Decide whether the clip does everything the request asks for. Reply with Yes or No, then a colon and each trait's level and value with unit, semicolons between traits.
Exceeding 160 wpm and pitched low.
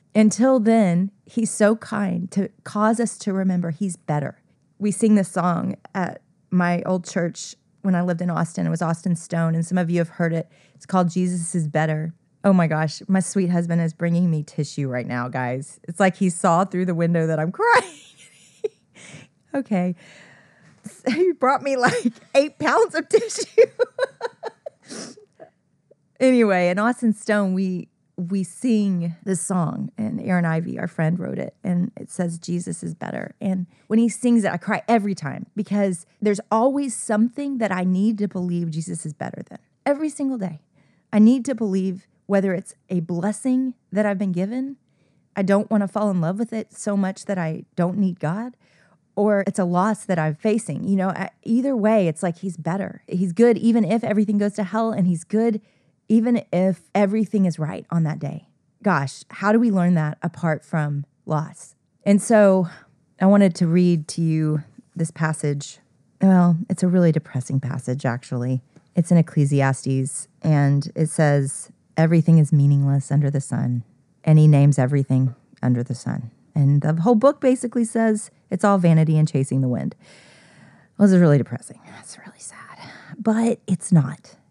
No: average, 180 wpm; medium, 185 Hz